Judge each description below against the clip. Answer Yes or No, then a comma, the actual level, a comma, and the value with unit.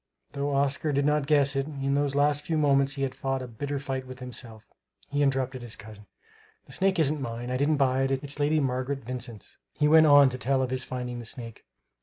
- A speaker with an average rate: No, fast, 225 wpm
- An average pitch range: No, narrow, 2.1 semitones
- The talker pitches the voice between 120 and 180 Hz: Yes, low, 135 Hz